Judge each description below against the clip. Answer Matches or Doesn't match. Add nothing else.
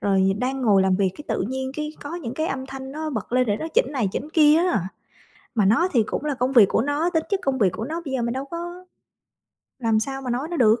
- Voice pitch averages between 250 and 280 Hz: Matches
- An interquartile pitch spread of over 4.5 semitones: Matches